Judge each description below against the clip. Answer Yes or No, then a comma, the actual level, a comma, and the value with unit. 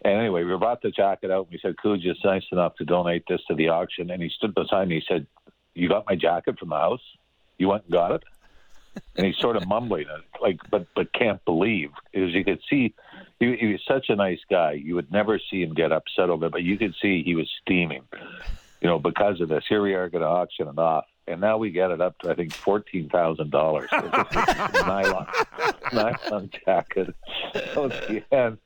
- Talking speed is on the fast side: Yes, fast, 220 wpm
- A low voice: Yes, very low, 95 Hz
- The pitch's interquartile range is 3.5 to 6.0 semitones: No, average, 2.8 semitones